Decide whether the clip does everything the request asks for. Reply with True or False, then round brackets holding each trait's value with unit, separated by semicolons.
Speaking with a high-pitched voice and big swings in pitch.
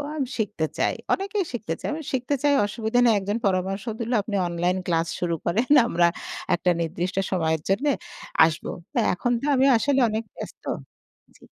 True (205 Hz; 6.0 semitones)